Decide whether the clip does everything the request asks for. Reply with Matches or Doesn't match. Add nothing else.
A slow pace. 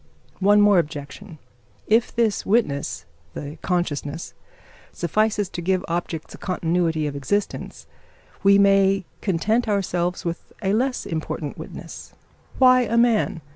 Matches